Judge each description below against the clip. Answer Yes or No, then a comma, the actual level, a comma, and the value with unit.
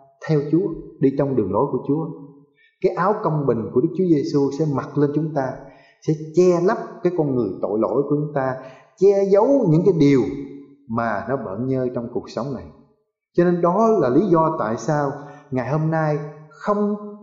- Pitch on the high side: No, medium, 150 Hz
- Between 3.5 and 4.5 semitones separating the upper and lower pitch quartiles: Yes, average, 4.1 semitones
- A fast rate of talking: No, average, 200 wpm